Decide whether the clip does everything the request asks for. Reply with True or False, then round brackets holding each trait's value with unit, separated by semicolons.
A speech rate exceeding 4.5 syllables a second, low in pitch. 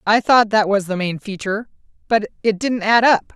False (5.2 syllables/s; 210 Hz)